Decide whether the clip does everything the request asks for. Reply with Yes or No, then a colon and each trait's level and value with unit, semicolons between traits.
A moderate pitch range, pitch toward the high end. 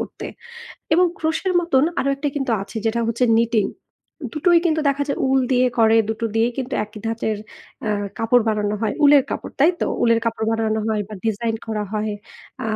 Yes: average, 3.9 semitones; high, 230 Hz